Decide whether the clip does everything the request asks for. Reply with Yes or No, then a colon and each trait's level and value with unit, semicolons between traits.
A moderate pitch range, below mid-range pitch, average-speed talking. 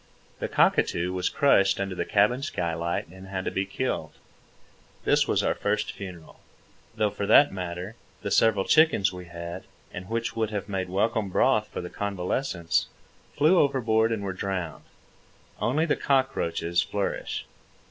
Yes: average, 3.7 semitones; low, 100 Hz; average, 150 wpm